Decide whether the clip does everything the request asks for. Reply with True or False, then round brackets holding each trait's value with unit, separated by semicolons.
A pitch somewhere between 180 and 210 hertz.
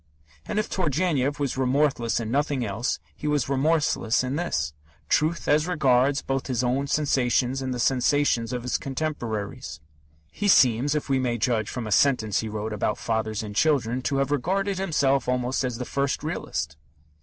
False (130 Hz)